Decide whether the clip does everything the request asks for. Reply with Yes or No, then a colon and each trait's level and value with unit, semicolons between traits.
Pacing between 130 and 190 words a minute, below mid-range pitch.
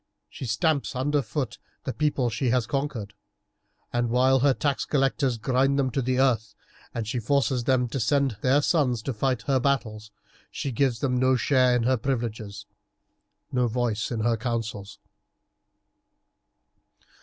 Yes: average, 155 wpm; low, 125 Hz